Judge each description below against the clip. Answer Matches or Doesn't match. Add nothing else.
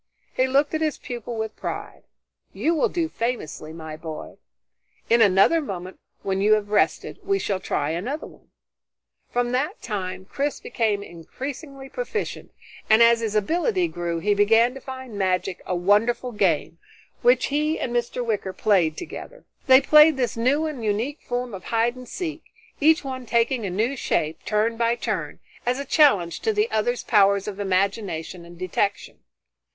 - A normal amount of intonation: Doesn't match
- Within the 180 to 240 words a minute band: Doesn't match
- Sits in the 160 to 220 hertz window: Doesn't match